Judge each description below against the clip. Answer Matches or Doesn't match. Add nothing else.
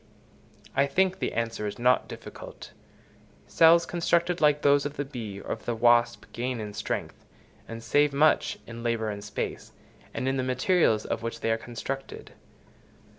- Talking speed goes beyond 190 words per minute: Doesn't match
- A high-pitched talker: Doesn't match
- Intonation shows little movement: Doesn't match